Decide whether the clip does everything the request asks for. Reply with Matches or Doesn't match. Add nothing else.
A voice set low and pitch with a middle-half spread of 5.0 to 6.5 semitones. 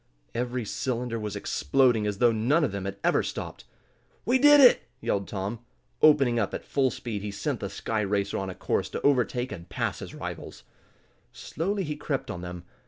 Matches